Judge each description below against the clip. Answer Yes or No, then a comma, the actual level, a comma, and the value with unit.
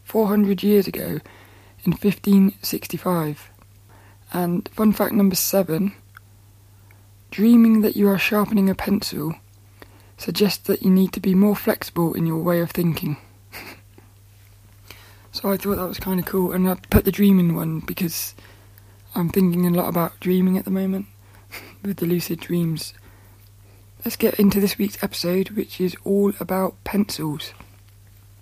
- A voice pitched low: No, medium, 170 Hz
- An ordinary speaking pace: Yes, average, 150 wpm